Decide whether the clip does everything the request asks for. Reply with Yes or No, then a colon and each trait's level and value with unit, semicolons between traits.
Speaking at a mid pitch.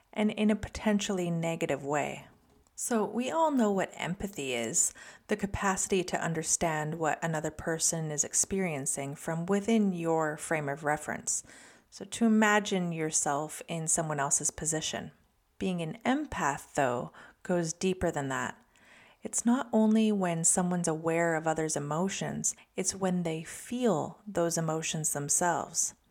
Yes: medium, 170 Hz